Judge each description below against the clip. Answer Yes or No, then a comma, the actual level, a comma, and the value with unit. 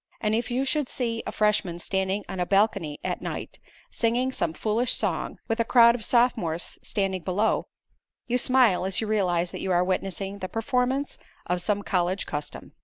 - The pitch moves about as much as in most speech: Yes, average, 4.2 semitones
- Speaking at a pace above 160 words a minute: Yes, average, 180 wpm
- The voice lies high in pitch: Yes, high, 210 Hz